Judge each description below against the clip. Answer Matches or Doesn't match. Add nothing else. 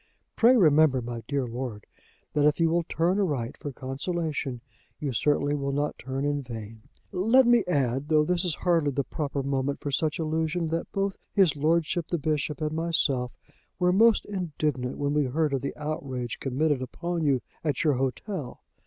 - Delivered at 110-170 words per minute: Doesn't match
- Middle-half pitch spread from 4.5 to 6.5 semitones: Doesn't match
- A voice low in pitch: Doesn't match